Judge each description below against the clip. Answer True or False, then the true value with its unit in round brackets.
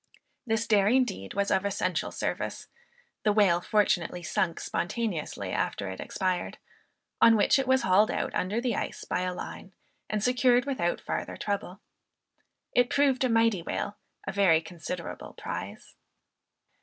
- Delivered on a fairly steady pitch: False (4.3 semitones)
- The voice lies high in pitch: True (200 Hz)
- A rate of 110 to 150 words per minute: True (145 wpm)